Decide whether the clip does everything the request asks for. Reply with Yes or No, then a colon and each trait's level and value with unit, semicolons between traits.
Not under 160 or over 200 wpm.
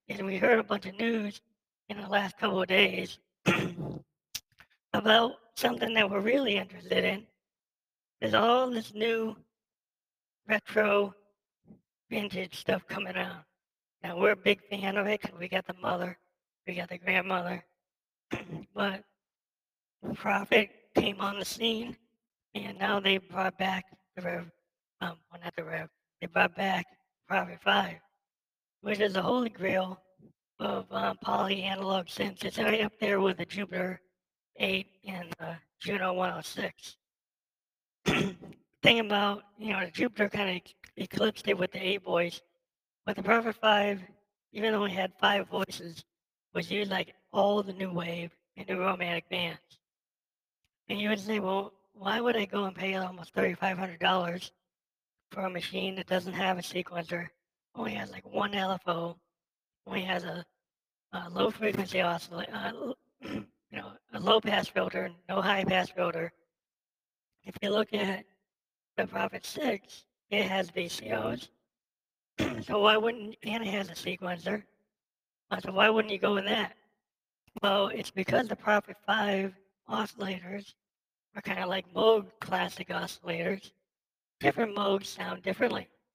No: average, 145 wpm